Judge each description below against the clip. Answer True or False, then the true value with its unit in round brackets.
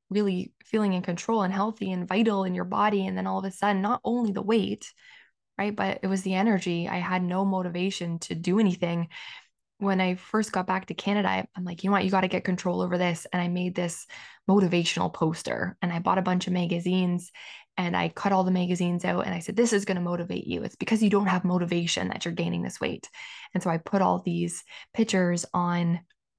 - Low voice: False (185 Hz)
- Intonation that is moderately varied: False (2.2 semitones)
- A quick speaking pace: True (230 wpm)